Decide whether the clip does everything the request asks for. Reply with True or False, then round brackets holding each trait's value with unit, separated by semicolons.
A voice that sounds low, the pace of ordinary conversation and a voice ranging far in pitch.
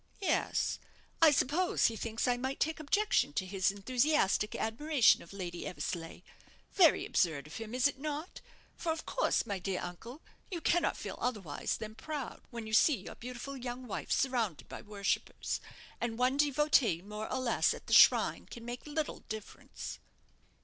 False (245 Hz; 170 wpm; 6.1 semitones)